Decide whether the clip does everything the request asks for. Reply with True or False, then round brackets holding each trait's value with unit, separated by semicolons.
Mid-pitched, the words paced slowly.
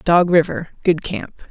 True (170 Hz; 120 wpm)